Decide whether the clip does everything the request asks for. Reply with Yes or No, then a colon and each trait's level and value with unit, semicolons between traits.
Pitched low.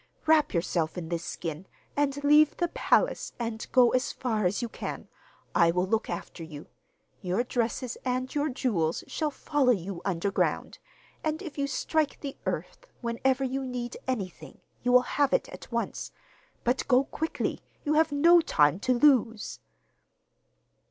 No: very high, 250 Hz